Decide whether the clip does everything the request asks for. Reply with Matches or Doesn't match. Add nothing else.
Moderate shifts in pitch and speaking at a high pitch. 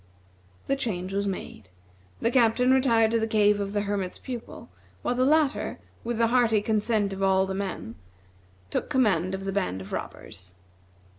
Matches